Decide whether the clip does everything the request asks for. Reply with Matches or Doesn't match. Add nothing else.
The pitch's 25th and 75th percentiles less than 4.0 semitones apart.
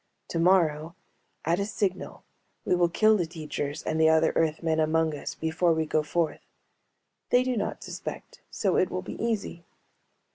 Matches